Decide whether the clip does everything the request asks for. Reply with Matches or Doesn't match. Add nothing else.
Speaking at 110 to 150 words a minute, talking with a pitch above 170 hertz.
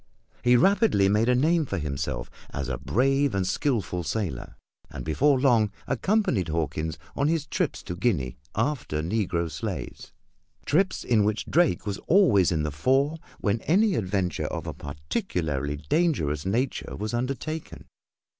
Doesn't match